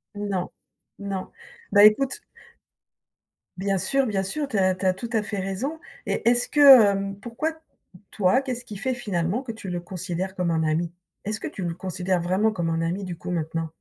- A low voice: No, high, 195 Hz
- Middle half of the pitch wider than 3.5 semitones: Yes, average, 3.9 semitones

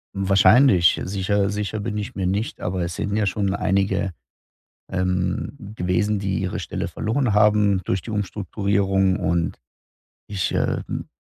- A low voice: Yes, low, 100 Hz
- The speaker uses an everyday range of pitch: No, narrow, 2.0 semitones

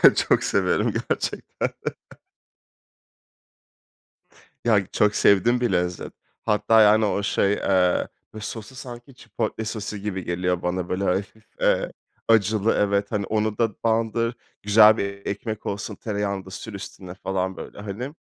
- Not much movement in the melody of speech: Yes, narrow, 2.3 semitones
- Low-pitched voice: Yes, low, 105 Hz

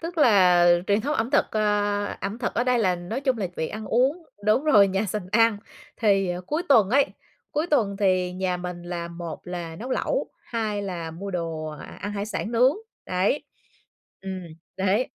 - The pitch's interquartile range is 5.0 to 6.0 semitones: No, average, 4.4 semitones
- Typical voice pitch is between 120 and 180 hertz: No, high, 205 Hz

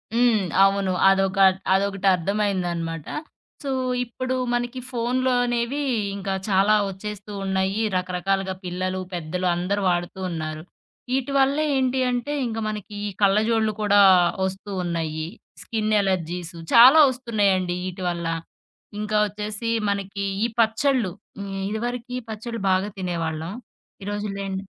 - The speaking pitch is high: Yes, high, 200 Hz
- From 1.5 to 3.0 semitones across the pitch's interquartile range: No, average, 3.7 semitones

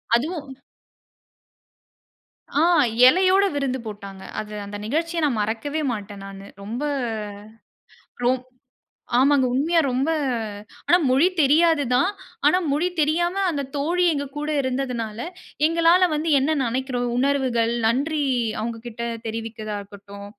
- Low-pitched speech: No, very high, 265 Hz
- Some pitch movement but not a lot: No, wide, 5.7 semitones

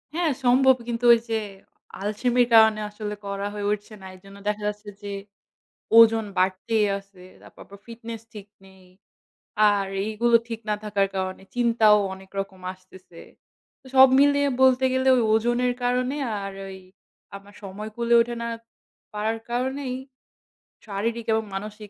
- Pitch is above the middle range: Yes, high, 220 Hz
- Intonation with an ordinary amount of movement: Yes, average, 3.2 semitones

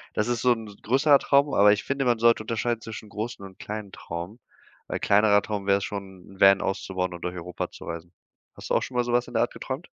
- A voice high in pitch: No, low, 105 Hz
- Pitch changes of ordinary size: Yes, average, 3.6 semitones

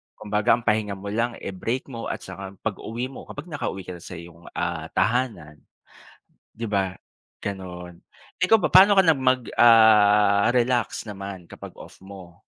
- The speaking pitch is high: No, low, 105 Hz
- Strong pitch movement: No, average, 4.2 semitones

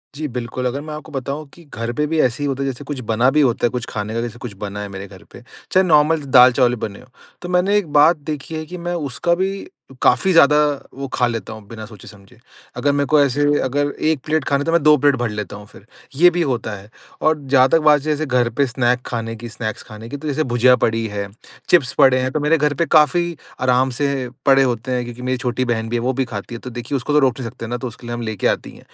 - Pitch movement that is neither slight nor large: Yes, average, 4.0 semitones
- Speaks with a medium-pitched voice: No, low, 130 Hz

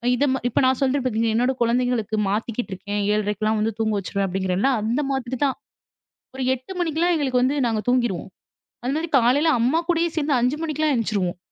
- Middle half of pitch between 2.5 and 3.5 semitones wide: No, average, 4.2 semitones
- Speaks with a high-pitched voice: Yes, high, 245 Hz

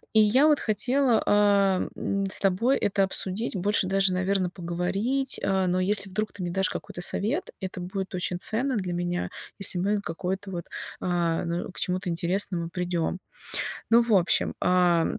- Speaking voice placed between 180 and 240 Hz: Yes, high, 190 Hz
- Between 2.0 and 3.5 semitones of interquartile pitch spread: Yes, average, 2.7 semitones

